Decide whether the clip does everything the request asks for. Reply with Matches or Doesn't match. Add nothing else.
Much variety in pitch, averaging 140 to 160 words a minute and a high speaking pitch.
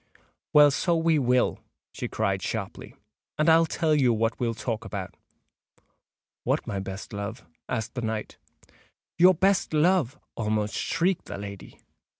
Doesn't match